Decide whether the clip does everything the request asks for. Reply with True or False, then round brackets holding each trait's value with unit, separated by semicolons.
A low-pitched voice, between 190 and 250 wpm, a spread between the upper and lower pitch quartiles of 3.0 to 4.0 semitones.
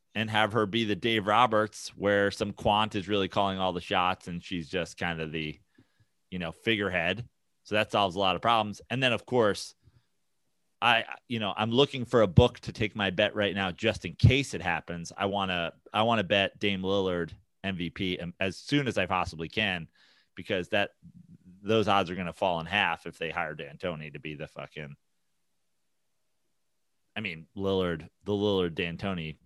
True (100 Hz; 200 wpm; 3.5 semitones)